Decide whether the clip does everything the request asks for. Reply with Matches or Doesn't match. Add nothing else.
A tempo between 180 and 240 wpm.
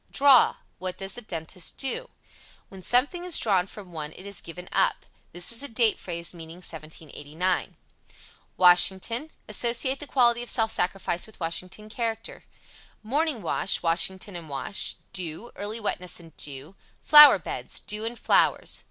Doesn't match